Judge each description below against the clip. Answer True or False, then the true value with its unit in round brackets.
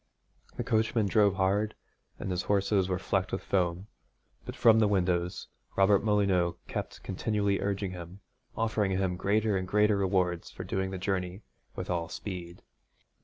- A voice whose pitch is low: True (95 Hz)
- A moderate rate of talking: True (160 wpm)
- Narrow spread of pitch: True (2.2 semitones)